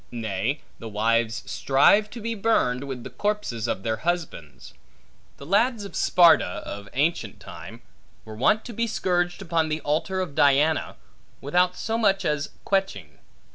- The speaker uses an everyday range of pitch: No, wide, 8.7 semitones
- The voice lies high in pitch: No, medium, 155 Hz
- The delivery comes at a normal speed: Yes, average, 155 wpm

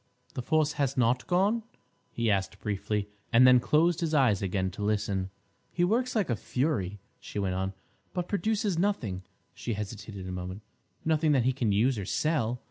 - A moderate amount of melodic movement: No, wide, 7.8 semitones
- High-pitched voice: No, low, 120 Hz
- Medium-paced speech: Yes, average, 170 wpm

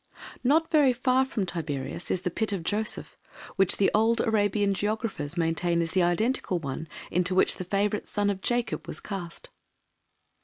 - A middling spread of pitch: Yes, average, 4.4 semitones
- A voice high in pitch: Yes, high, 200 Hz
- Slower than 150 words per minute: No, average, 160 wpm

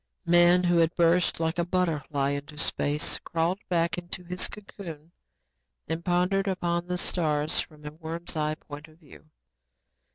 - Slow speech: No, average, 155 wpm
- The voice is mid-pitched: Yes, medium, 170 Hz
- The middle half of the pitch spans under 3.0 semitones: Yes, narrow, 2.4 semitones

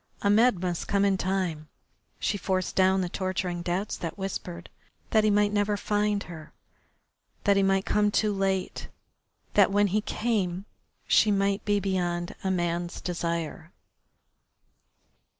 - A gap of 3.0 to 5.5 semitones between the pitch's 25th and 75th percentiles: No, narrow, 2.5 semitones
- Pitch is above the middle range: Yes, high, 195 Hz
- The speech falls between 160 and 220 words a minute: No, average, 140 wpm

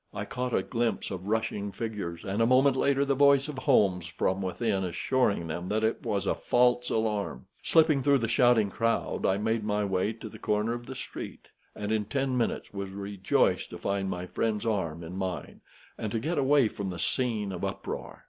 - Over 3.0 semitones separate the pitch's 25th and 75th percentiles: Yes, average, 4.2 semitones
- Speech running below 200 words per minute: No, fast, 205 wpm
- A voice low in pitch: Yes, low, 110 Hz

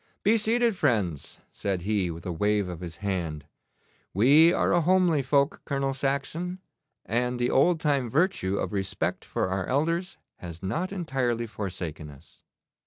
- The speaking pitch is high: No, low, 125 Hz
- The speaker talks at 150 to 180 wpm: Yes, average, 155 wpm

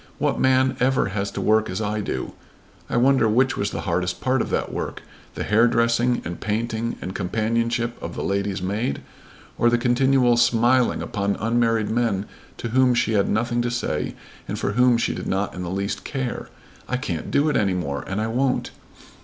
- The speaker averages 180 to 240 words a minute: Yes, average, 195 wpm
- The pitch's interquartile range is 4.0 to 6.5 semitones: No, average, 3.3 semitones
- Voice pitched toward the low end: Yes, low, 115 Hz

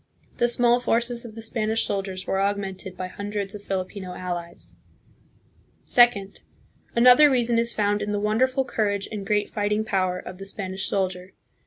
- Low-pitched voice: No, high, 205 Hz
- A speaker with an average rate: Yes, average, 165 wpm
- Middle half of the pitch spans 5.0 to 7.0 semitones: No, average, 3.2 semitones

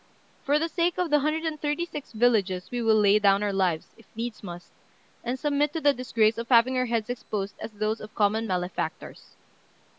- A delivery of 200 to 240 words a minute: Yes, fast, 205 wpm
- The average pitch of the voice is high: Yes, high, 230 Hz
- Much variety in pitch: Yes, wide, 5.7 semitones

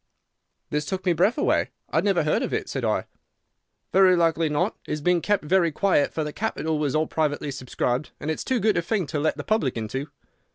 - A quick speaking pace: Yes, fast, 220 wpm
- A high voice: No, medium, 160 Hz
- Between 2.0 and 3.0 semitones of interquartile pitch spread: No, average, 4.2 semitones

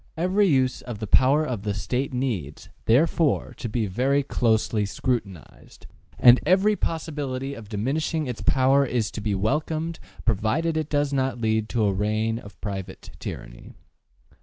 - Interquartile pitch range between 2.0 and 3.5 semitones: No, average, 5.1 semitones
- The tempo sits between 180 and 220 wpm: No, average, 155 wpm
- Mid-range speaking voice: No, low, 125 Hz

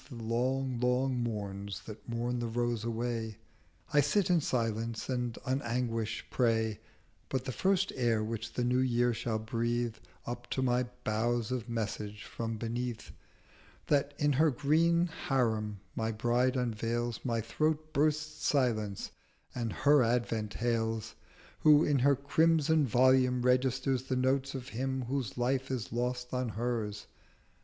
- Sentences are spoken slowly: No, average, 150 wpm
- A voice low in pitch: Yes, low, 120 Hz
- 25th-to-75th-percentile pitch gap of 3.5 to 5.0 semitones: No, narrow, 2.6 semitones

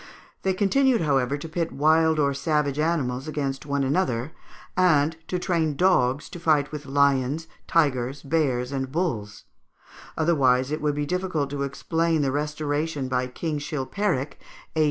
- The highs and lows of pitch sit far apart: No, average, 3.2 semitones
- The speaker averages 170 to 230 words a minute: No, average, 150 wpm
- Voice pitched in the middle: Yes, medium, 150 Hz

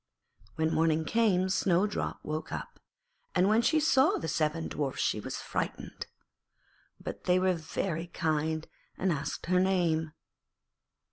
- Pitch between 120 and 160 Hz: No, medium, 170 Hz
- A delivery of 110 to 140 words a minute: Yes, slow, 135 wpm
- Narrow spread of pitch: No, average, 3.0 semitones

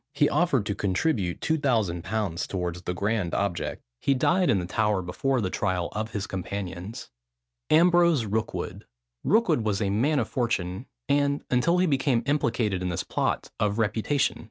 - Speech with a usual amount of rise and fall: No, wide, 6.6 semitones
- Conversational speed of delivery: Yes, average, 155 wpm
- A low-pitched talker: Yes, low, 110 Hz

